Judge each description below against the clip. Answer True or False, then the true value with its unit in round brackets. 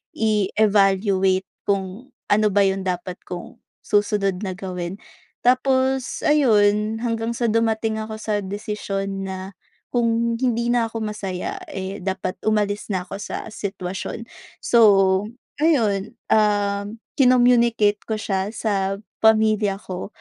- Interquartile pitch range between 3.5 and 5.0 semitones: False (2.8 semitones)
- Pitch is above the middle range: True (210 Hz)